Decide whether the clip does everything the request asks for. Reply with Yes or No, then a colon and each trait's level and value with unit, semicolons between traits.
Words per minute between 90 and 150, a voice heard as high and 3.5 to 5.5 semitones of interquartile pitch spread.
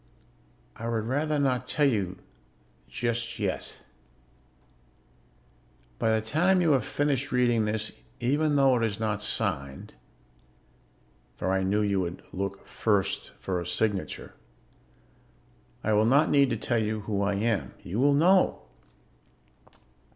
No: slow, 135 wpm; low, 110 Hz; average, 5.2 semitones